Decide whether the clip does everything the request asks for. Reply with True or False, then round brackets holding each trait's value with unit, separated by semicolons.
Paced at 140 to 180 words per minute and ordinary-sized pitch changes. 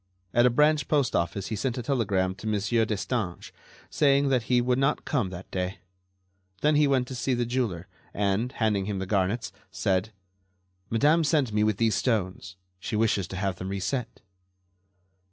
True (170 wpm; 4.9 semitones)